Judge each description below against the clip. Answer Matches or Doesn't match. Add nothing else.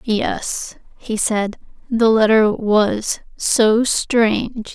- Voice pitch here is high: Matches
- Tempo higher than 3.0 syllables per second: Doesn't match